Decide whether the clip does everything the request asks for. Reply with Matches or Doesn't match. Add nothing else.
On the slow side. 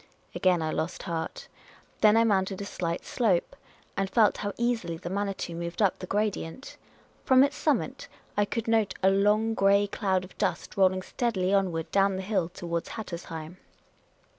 Doesn't match